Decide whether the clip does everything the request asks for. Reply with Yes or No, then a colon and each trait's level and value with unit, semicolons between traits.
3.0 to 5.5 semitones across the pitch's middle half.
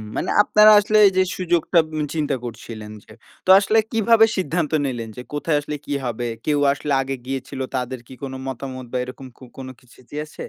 Yes: average, 4.9 semitones